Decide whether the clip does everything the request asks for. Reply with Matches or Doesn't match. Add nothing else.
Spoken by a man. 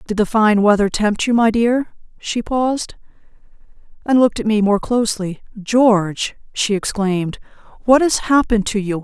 Doesn't match